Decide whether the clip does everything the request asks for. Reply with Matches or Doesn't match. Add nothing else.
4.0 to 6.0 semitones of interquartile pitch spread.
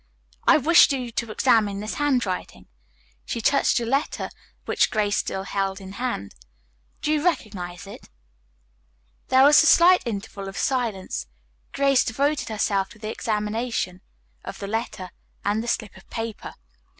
Matches